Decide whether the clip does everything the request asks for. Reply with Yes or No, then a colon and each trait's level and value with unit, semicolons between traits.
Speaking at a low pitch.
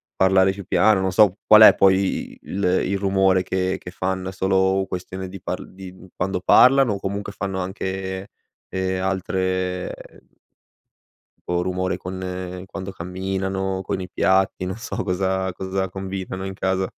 Yes: very low, 95 Hz